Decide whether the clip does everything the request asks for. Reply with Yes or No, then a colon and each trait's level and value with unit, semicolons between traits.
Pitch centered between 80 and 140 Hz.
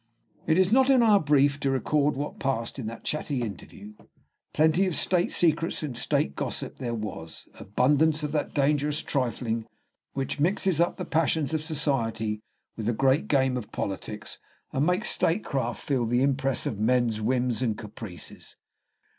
Yes: low, 135 Hz